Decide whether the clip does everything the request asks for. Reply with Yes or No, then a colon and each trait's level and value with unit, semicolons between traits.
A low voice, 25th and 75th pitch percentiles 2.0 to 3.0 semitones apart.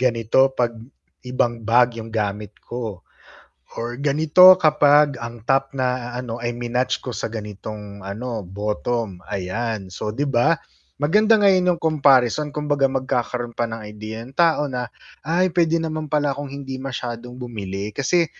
No: low, 125 Hz; average, 4.3 semitones